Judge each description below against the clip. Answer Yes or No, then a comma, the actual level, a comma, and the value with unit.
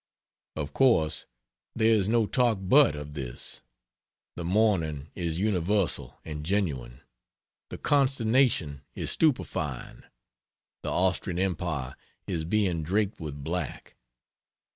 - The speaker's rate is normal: No, slow, 110 wpm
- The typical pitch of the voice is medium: No, very low, 90 Hz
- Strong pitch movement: Yes, wide, 6.0 semitones